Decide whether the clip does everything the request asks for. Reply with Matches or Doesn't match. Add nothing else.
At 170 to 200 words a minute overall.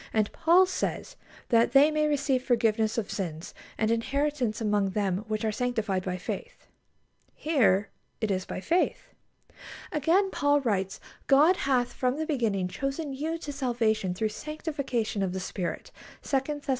Doesn't match